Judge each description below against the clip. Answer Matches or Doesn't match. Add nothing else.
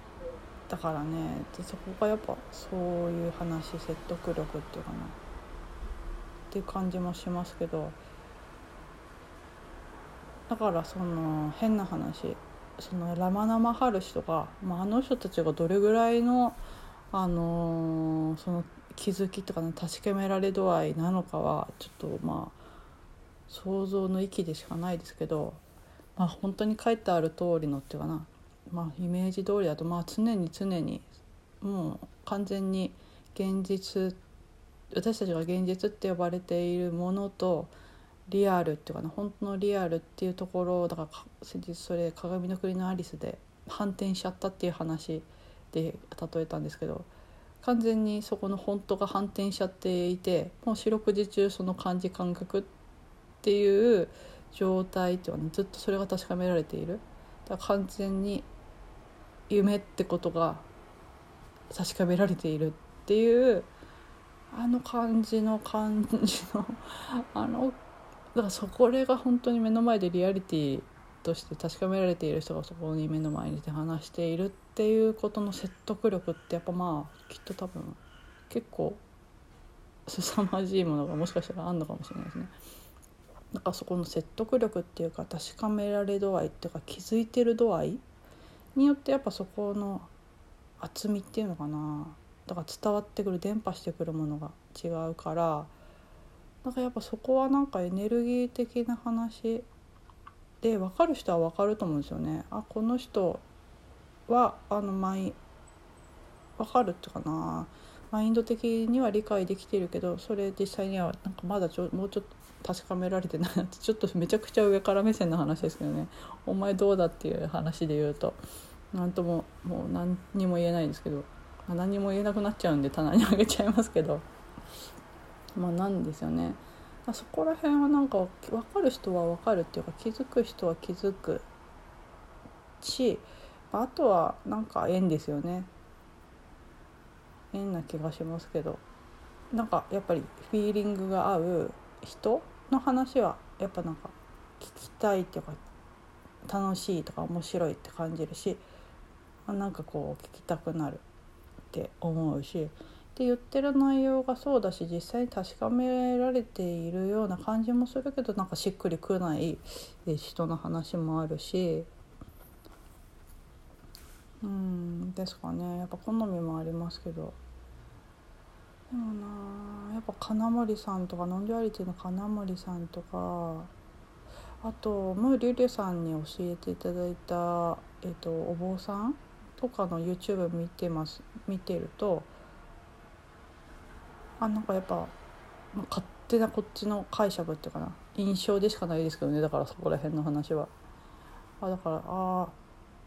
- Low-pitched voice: Doesn't match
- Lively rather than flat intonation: Doesn't match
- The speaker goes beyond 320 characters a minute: Doesn't match